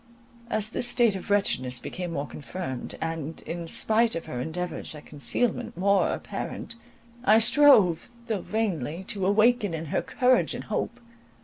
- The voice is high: Yes, high, 195 Hz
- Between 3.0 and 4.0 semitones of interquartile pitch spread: No, wide, 5.6 semitones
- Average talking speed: Yes, average, 150 wpm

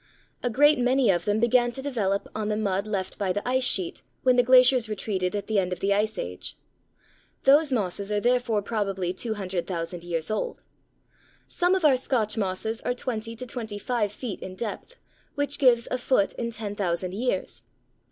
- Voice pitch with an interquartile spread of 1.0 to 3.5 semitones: No, average, 4.2 semitones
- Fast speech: No, average, 180 wpm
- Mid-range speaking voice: No, high, 215 Hz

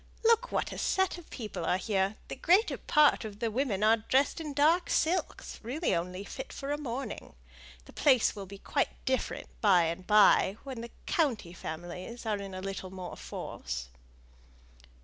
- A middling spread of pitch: No, wide, 7.0 semitones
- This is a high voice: Yes, high, 220 Hz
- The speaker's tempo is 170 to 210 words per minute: Yes, average, 175 wpm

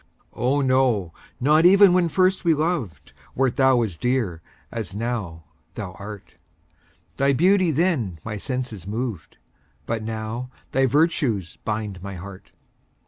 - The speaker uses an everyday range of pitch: No, wide, 6.0 semitones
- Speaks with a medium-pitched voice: No, low, 120 Hz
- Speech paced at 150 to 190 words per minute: No, slow, 135 wpm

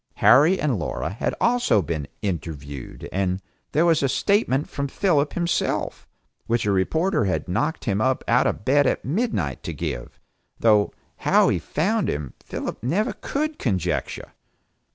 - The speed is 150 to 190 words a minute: Yes, average, 155 wpm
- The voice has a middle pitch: No, low, 130 Hz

